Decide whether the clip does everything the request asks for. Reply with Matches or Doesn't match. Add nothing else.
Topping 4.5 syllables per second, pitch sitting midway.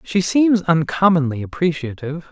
Matches